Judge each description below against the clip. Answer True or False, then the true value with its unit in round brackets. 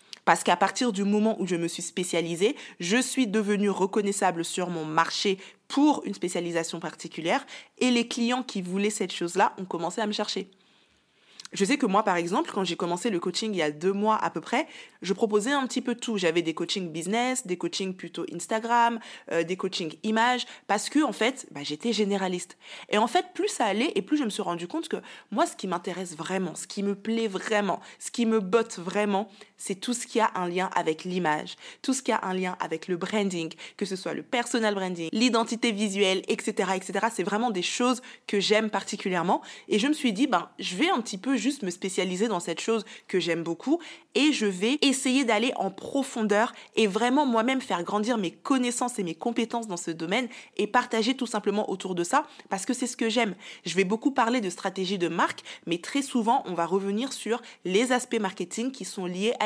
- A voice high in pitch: True (210 Hz)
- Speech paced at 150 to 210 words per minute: False (220 wpm)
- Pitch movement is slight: False (4.6 semitones)